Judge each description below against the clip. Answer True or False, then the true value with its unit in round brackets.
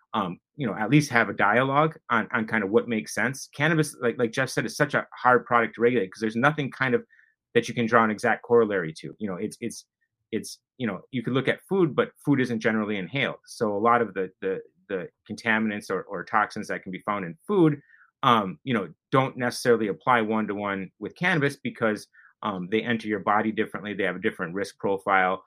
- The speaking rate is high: True (225 wpm)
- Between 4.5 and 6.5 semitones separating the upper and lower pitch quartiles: True (5.0 semitones)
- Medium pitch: False (120 Hz)